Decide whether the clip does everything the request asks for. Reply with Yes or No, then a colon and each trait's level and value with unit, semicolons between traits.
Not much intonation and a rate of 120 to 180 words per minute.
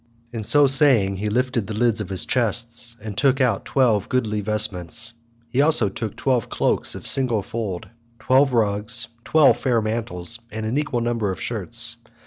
No: average, 3.0 semitones; average, 165 wpm